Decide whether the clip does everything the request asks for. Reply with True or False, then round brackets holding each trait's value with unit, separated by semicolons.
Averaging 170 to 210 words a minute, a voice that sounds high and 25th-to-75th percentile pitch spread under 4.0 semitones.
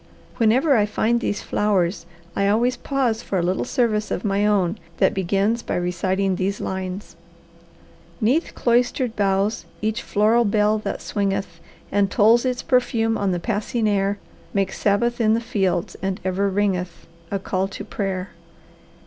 False (155 wpm; 205 Hz; 2.8 semitones)